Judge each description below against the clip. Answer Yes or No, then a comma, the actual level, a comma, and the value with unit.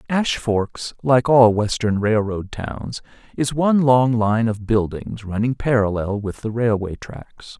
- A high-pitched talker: No, low, 115 Hz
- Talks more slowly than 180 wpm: Yes, average, 150 wpm